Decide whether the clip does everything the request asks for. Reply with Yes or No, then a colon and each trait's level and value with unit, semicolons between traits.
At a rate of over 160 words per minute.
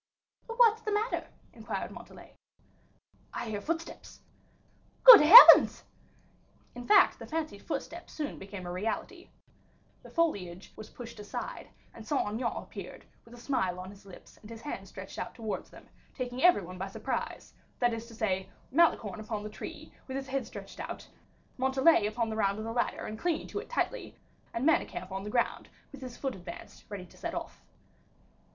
Yes: average, 175 wpm